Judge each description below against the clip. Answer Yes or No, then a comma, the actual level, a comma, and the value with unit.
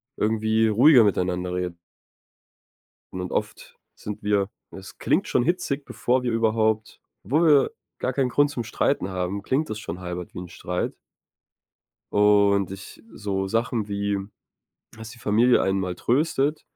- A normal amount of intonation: Yes, average, 4.3 semitones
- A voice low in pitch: Yes, low, 105 Hz